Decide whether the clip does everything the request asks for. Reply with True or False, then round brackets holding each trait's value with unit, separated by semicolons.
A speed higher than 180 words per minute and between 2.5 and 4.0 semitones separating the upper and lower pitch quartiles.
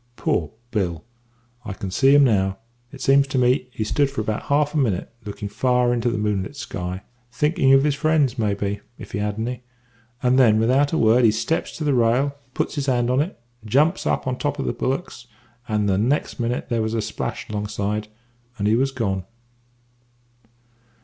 False (200 wpm; 4.5 semitones)